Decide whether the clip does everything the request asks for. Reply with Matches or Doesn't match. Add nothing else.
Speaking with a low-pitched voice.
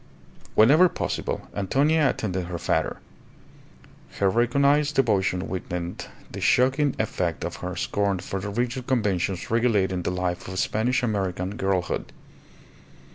Matches